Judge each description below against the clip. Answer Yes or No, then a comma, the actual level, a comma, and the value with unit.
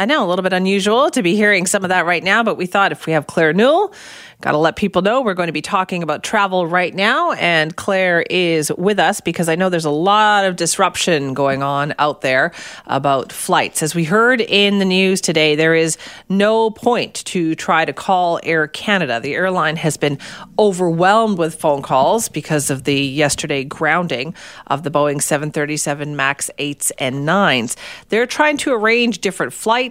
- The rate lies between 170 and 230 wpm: Yes, average, 200 wpm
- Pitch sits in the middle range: Yes, medium, 175 Hz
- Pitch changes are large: No, average, 4.8 semitones